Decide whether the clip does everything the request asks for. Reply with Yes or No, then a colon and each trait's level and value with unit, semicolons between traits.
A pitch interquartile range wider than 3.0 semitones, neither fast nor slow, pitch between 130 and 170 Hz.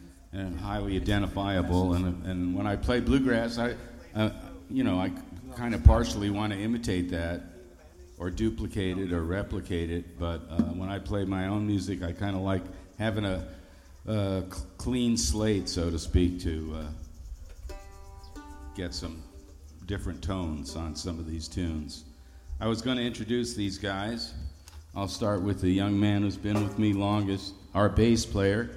No: average, 3.5 semitones; average, 165 wpm; very low, 95 Hz